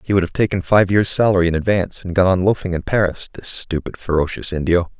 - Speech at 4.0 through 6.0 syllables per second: No, 6.3 syllables/s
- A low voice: Yes, very low, 90 Hz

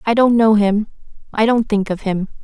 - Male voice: No, female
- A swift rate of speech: Yes, fast, 220 wpm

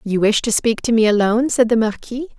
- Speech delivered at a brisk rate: Yes, fast, 250 wpm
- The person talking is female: Yes, female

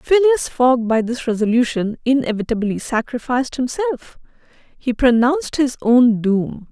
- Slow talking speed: Yes, slow, 115 wpm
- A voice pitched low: No, very high, 250 Hz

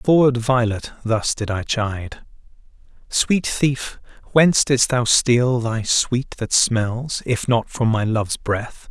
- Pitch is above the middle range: No, low, 120 Hz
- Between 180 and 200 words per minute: No, average, 155 wpm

